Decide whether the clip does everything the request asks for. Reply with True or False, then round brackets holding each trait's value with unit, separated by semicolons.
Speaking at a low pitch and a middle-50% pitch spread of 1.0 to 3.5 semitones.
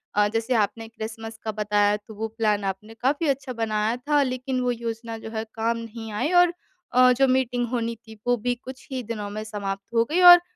False (230 Hz; 2.6 semitones)